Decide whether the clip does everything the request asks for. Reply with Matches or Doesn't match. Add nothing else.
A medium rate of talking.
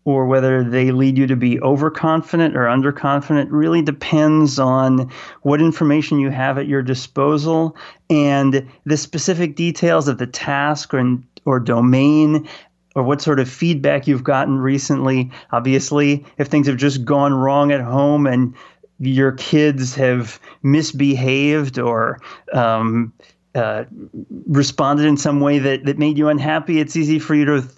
Matches